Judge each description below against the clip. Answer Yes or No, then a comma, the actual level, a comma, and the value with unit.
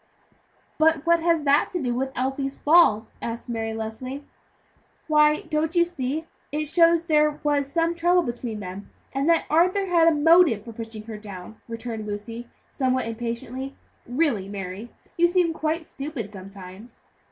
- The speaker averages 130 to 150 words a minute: No, average, 160 wpm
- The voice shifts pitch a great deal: Yes, wide, 6.2 semitones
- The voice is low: No, very high, 270 Hz